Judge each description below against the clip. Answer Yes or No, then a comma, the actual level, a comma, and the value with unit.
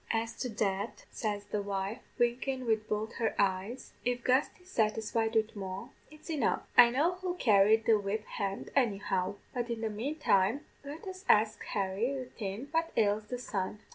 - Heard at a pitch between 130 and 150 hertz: No, high, 225 Hz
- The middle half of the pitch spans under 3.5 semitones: No, average, 3.8 semitones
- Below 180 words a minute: Yes, average, 170 wpm